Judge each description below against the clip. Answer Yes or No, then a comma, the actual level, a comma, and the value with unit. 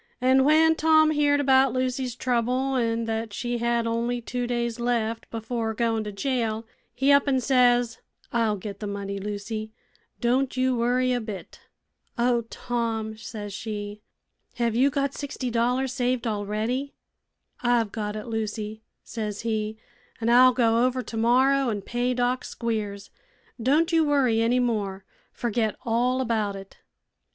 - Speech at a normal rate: Yes, average, 150 wpm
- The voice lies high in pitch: Yes, high, 235 Hz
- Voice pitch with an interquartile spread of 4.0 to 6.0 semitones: No, narrow, 2.6 semitones